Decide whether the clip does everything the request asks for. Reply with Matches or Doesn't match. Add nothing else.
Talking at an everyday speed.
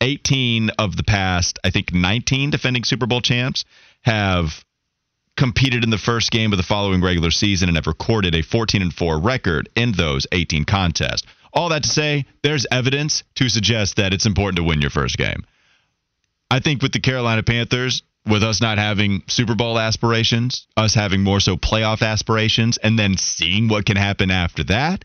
Matches